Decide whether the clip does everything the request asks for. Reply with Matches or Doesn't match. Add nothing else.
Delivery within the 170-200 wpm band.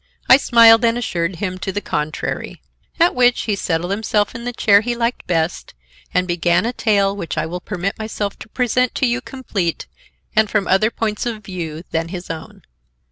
Matches